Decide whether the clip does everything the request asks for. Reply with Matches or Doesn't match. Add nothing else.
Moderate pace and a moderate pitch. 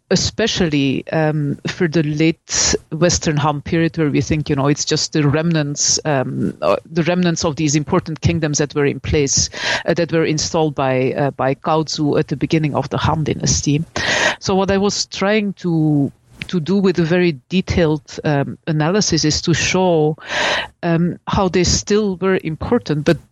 Matches